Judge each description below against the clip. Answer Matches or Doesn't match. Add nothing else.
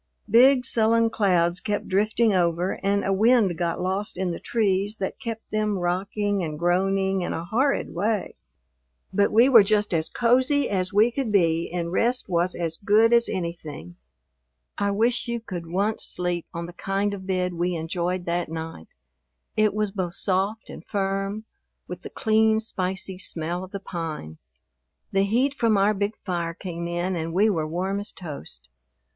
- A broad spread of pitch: Doesn't match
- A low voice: Doesn't match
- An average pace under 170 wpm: Doesn't match